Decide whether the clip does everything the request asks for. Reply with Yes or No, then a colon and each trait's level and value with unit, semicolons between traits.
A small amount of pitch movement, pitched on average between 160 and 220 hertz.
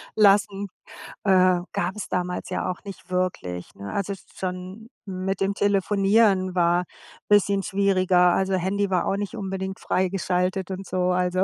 Yes: narrow, 1.5 semitones; high, 190 Hz